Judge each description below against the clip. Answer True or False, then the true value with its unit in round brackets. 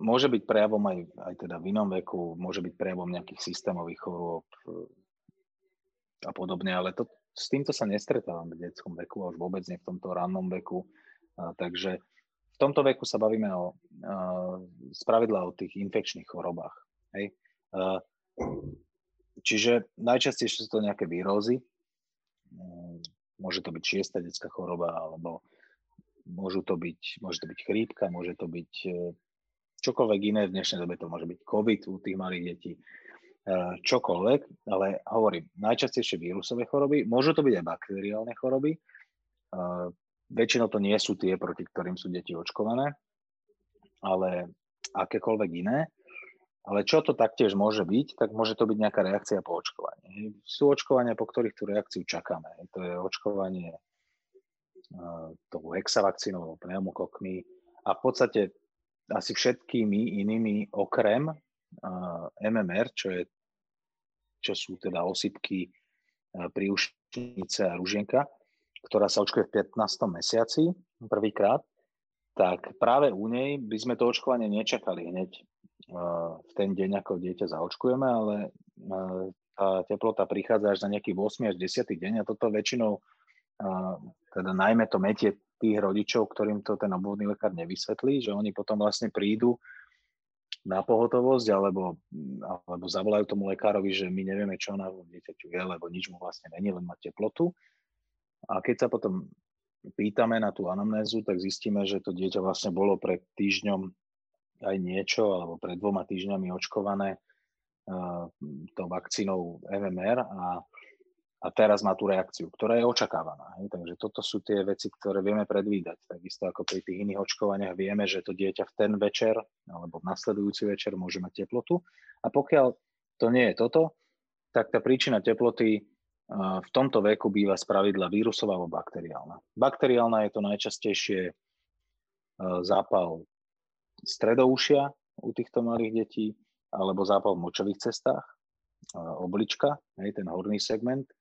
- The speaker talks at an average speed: True (145 wpm)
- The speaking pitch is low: True (100 Hz)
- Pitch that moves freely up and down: False (3.6 semitones)